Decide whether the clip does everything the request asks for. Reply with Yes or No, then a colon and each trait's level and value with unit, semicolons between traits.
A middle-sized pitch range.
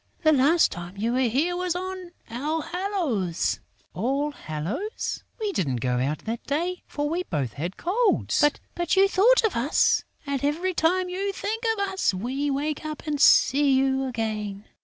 No: wide, 8.1 semitones